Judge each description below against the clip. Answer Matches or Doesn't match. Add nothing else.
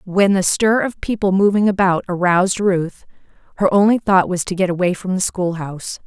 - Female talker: Matches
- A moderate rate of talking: Matches